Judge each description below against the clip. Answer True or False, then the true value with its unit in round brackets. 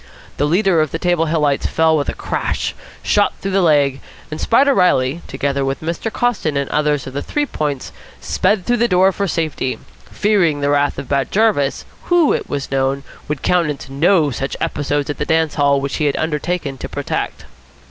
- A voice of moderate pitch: True (150 Hz)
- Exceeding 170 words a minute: True (195 wpm)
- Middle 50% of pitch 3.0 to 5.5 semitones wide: True (4.3 semitones)